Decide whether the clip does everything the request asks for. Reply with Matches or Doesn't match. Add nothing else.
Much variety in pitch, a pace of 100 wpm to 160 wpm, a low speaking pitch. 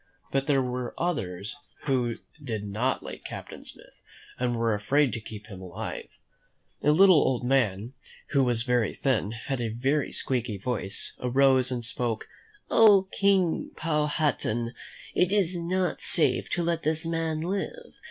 Matches